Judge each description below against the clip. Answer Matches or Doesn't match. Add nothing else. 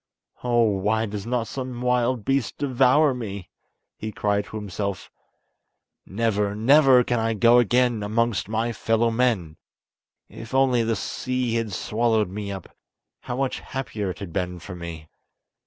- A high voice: Doesn't match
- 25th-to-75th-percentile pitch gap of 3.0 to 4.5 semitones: Matches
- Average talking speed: Matches